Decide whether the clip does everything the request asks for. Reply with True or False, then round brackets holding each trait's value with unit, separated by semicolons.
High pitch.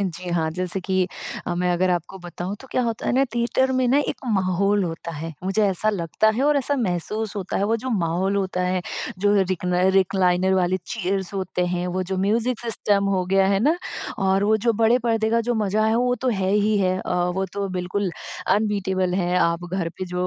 True (195 Hz)